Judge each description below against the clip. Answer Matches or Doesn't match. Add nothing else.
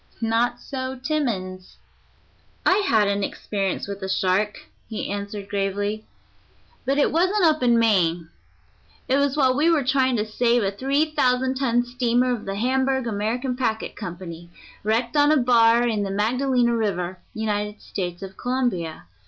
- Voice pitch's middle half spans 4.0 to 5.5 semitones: Matches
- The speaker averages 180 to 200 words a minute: Doesn't match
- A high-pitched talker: Matches